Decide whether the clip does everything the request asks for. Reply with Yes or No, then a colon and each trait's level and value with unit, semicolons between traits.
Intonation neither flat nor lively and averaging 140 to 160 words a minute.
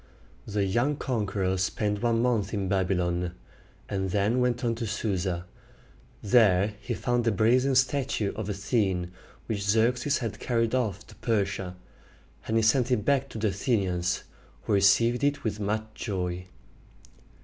Yes: average, 3.8 semitones; average, 150 wpm